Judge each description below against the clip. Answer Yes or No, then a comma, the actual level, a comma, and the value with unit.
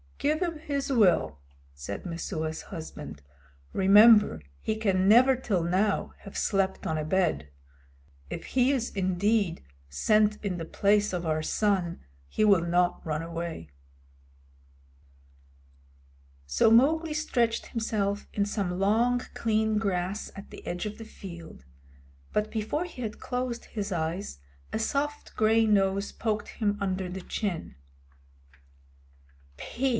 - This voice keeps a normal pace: No, slow, 130 wpm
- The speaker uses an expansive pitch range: No, average, 4.2 semitones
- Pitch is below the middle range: No, high, 200 Hz